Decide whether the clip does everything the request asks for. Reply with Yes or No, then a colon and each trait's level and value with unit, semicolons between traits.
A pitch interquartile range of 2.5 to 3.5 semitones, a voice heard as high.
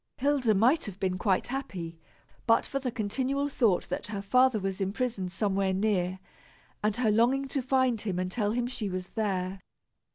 No: average, 4.9 semitones; high, 215 Hz